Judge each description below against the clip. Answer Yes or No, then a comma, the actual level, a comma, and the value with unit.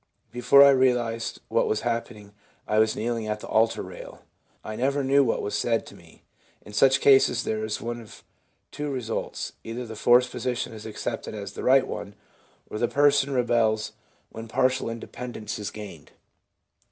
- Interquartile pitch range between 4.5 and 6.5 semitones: No, average, 2.8 semitones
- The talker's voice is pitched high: No, low, 115 Hz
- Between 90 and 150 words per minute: No, average, 175 wpm